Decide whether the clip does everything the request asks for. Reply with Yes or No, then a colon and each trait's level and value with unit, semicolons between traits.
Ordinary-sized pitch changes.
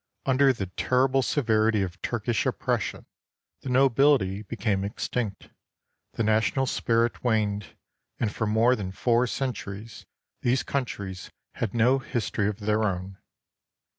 Yes: average, 3.7 semitones